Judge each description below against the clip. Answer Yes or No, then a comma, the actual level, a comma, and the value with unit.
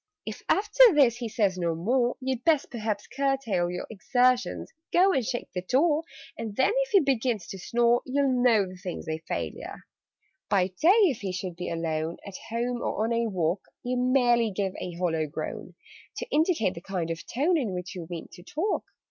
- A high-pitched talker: Yes, high, 230 Hz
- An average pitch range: No, wide, 6.3 semitones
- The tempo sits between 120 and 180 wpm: No, average, 195 wpm